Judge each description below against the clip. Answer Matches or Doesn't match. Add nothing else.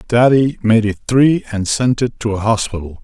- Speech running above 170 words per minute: Matches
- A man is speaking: Matches